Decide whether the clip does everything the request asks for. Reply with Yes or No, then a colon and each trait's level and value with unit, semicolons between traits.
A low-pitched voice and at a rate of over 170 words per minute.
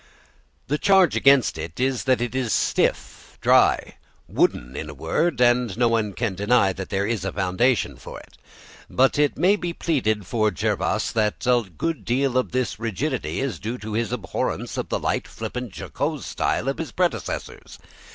Yes: low, 120 Hz; average, 180 wpm